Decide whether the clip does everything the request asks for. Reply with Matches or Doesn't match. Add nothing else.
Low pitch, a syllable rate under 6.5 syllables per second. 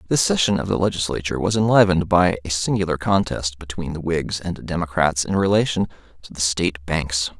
Matches